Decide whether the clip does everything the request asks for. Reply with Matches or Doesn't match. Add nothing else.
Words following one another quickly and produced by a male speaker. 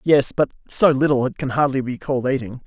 Matches